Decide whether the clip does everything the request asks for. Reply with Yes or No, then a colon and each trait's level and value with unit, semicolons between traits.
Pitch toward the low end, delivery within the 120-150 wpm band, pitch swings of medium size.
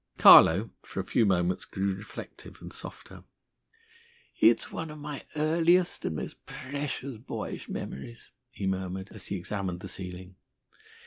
No: low, 100 Hz; average, 140 wpm; wide, 7.3 semitones